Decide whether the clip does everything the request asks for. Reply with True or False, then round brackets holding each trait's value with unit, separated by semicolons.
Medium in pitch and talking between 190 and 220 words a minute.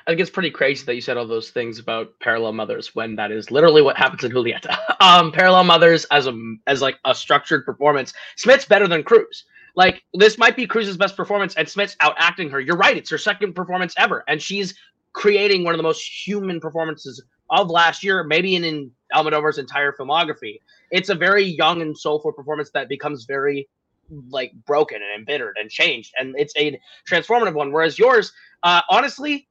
True (165 Hz; 200 wpm)